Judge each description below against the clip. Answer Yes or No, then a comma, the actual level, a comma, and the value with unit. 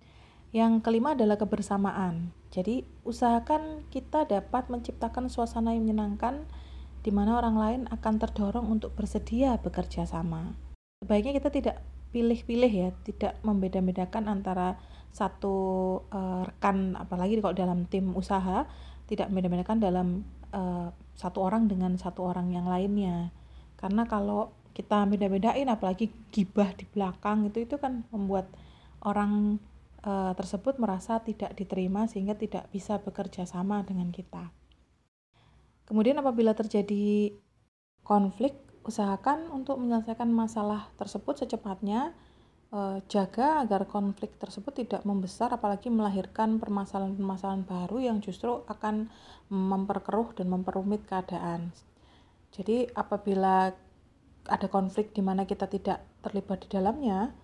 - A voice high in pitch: Yes, high, 205 Hz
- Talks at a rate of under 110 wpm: No, average, 115 wpm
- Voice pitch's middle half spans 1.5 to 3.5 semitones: Yes, average, 2.9 semitones